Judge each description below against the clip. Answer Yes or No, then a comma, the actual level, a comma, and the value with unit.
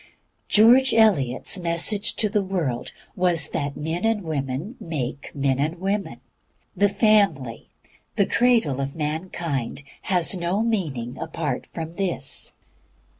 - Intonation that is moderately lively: No, wide, 6.2 semitones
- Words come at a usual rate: No, slow, 125 wpm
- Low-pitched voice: No, medium, 170 Hz